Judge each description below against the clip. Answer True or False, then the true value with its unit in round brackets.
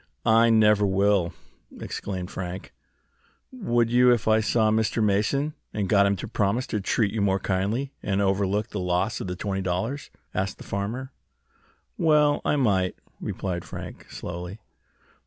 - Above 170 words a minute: False (155 wpm)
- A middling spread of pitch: True (3.2 semitones)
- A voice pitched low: True (105 Hz)